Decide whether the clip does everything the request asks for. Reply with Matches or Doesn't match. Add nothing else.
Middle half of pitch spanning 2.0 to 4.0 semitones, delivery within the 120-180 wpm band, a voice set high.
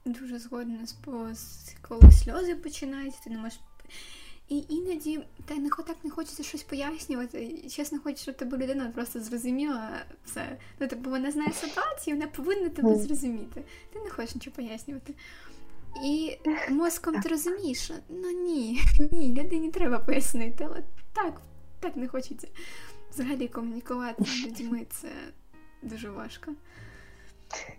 Doesn't match